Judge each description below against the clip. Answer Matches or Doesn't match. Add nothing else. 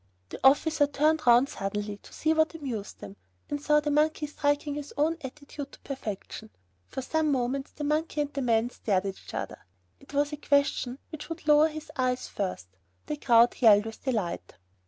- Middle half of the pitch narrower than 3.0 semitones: Doesn't match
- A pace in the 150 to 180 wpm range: Doesn't match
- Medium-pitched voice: Doesn't match